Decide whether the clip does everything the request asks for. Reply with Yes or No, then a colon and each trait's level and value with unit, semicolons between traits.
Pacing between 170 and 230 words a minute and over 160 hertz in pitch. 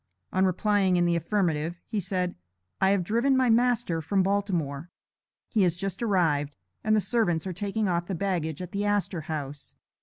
Yes: average, 180 wpm; medium, 185 Hz